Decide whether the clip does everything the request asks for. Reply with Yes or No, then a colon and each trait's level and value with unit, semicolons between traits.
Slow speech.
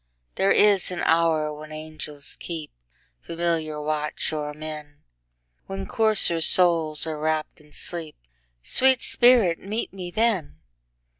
Yes: slow, 105 wpm